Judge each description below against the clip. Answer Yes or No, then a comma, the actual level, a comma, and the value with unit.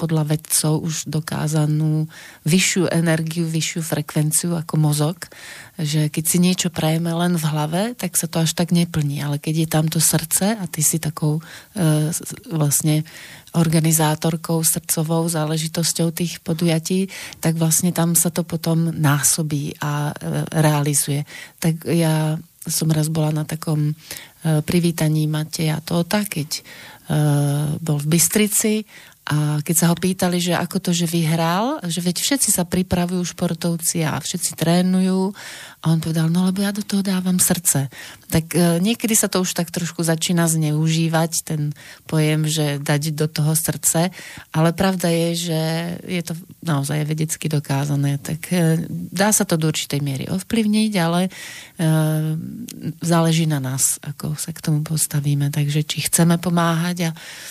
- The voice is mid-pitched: Yes, medium, 165 Hz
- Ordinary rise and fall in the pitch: No, narrow, 2.2 semitones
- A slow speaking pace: No, average, 150 wpm